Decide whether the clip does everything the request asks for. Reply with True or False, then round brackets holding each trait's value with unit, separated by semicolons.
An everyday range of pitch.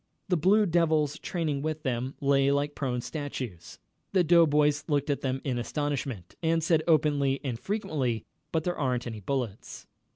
True (3.4 semitones)